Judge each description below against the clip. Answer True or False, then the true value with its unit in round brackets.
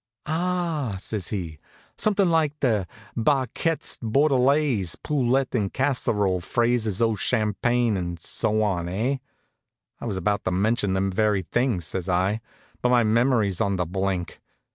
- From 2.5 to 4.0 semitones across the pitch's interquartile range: False (5.3 semitones)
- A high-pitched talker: False (110 Hz)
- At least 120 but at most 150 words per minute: True (135 wpm)